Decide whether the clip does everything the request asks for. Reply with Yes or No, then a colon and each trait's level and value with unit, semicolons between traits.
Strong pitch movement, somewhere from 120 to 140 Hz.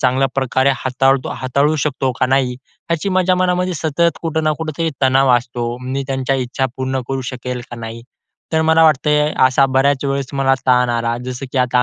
No: average, 2.8 semitones; low, 135 Hz